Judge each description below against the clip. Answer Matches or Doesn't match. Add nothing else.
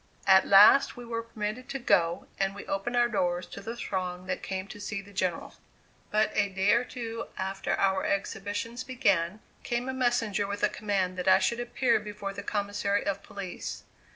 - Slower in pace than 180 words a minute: Doesn't match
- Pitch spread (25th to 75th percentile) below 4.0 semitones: Matches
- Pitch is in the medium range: Doesn't match